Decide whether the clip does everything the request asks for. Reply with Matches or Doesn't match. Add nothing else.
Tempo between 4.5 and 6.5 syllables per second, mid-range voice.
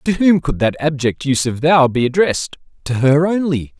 Matches